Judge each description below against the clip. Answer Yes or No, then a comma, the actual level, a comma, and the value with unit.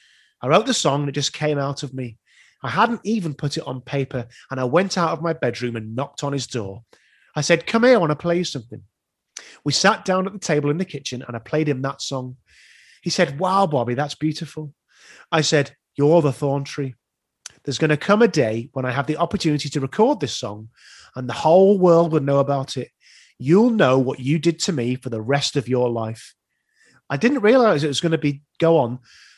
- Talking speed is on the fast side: Yes, fast, 230 wpm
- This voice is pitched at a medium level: Yes, medium, 145 Hz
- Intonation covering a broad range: No, average, 4.6 semitones